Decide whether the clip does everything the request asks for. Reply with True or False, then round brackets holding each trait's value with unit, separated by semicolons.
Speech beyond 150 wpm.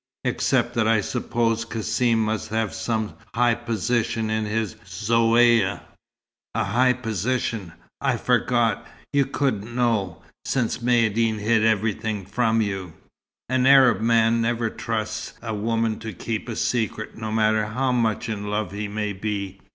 False (145 wpm)